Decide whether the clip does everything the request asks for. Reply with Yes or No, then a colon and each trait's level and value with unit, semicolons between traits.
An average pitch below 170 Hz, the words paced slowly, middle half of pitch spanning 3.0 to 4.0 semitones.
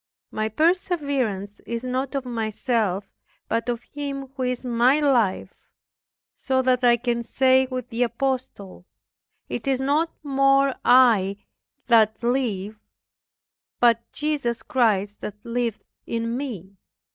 No: high, 245 Hz; slow, 120 wpm; average, 3.3 semitones